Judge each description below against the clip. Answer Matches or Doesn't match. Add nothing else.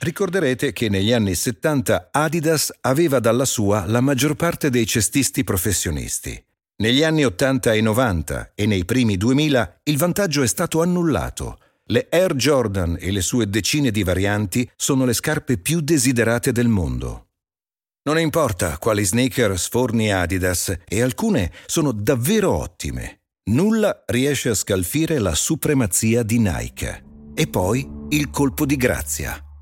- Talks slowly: Doesn't match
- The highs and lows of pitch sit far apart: Matches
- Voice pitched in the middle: Doesn't match